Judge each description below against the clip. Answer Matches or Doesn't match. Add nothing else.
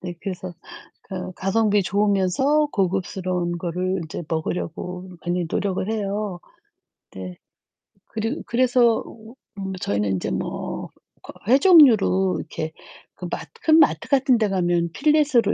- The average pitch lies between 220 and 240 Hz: Doesn't match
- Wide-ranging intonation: Doesn't match